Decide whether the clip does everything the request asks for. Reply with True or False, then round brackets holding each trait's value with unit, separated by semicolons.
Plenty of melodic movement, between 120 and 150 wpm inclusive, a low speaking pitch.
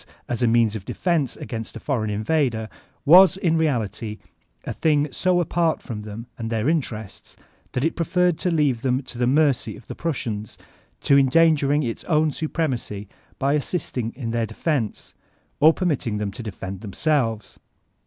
False (5.9 semitones; 165 wpm; 130 Hz)